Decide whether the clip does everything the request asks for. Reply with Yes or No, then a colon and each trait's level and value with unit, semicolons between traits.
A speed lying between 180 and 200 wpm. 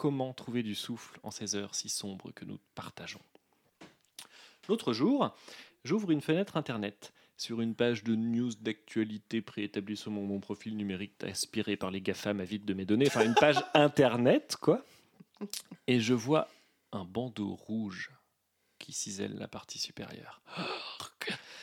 No: average, 155 wpm